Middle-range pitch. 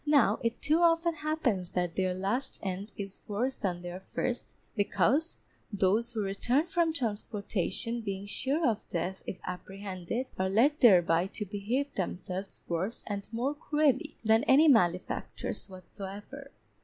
No: high, 210 Hz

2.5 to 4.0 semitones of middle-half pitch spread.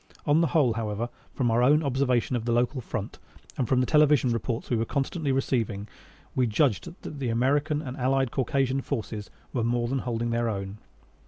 Yes: average, 2.9 semitones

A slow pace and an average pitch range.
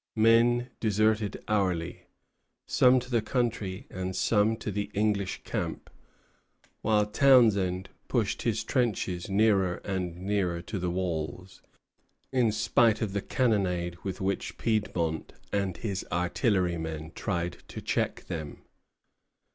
Yes: slow, 120 wpm; average, 3.5 semitones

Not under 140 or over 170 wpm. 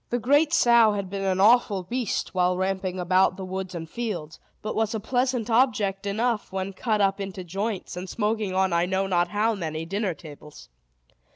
No: average, 190 wpm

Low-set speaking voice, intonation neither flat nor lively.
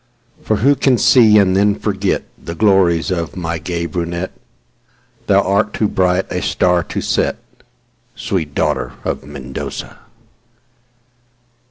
Yes: very low, 95 Hz; average, 3.3 semitones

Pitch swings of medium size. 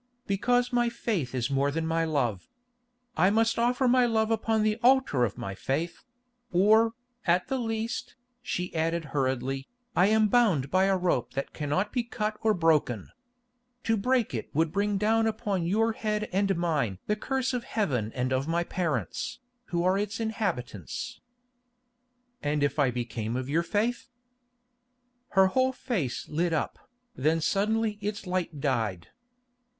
No: wide, 7.4 semitones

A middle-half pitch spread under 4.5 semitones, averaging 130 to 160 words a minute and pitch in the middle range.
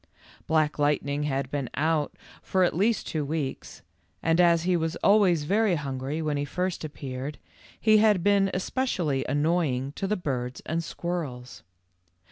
Yes: average, 4.1 semitones; average, 150 wpm; medium, 160 Hz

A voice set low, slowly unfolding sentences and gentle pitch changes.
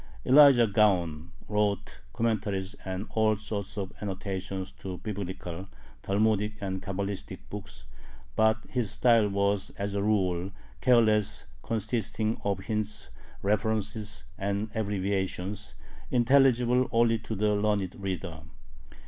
Yes: low, 105 Hz; slow, 110 wpm; narrow, 2.2 semitones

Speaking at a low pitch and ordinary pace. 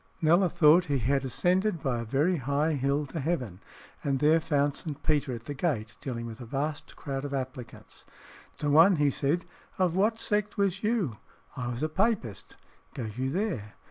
No: medium, 145 Hz; average, 185 wpm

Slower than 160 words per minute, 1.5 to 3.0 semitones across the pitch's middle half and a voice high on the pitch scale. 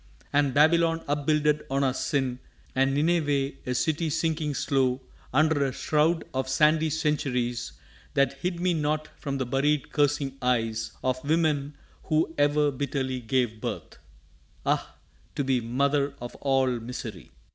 No: average, 140 wpm; average, 2.7 semitones; medium, 140 Hz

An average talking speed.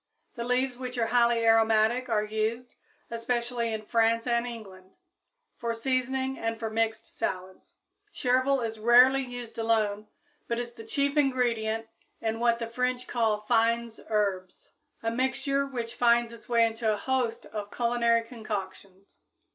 Yes: average, 145 wpm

